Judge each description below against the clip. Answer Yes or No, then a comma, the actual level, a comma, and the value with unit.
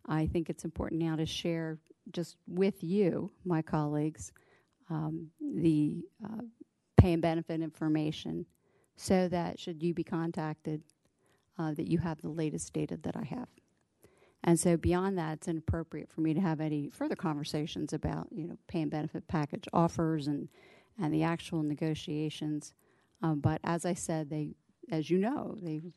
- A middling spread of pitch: No, narrow, 1.8 semitones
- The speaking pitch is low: No, medium, 165 Hz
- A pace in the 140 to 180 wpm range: Yes, average, 165 wpm